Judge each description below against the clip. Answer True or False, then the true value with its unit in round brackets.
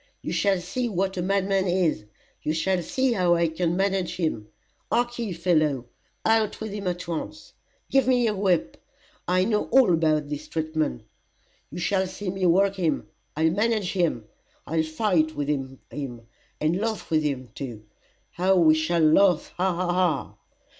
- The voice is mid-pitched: True (180 Hz)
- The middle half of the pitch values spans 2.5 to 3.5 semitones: False (3.9 semitones)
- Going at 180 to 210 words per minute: False (165 wpm)